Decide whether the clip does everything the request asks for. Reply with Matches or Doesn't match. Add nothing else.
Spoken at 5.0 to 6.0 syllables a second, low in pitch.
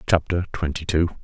Matches